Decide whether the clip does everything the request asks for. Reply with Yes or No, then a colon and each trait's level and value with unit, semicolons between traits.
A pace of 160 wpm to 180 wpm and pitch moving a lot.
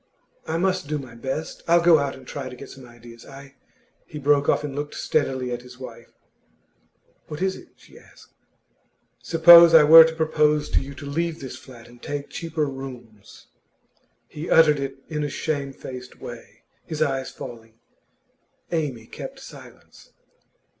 No: average, 165 wpm; average, 3.6 semitones